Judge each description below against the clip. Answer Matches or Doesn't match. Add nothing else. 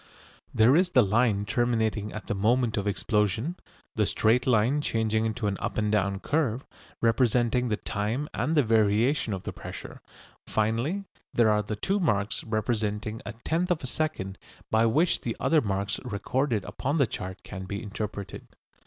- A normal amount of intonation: Matches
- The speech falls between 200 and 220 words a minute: Doesn't match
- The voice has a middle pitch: Doesn't match